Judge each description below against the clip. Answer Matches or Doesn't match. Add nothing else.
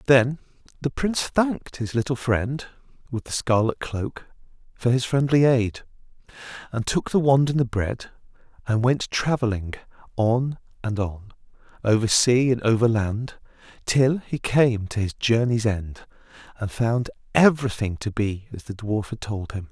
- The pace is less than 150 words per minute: Doesn't match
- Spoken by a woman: Doesn't match